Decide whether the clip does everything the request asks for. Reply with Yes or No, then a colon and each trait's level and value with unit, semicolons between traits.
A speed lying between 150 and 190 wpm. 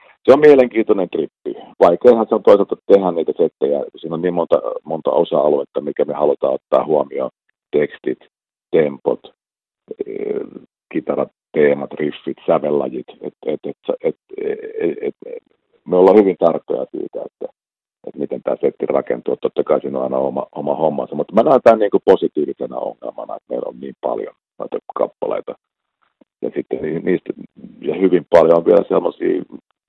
Yes: fast, 155 wpm